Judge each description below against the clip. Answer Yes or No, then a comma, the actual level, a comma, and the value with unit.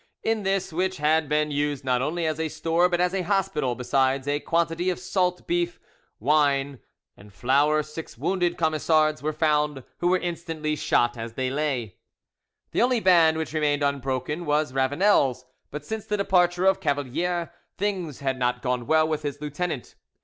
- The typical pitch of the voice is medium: Yes, medium, 155 Hz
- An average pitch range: Yes, average, 3.9 semitones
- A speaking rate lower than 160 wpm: No, average, 170 wpm